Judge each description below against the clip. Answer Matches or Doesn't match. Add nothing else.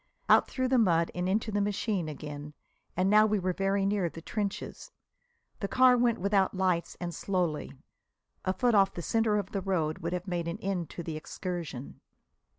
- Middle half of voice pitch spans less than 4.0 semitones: Matches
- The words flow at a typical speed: Matches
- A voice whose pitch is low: Doesn't match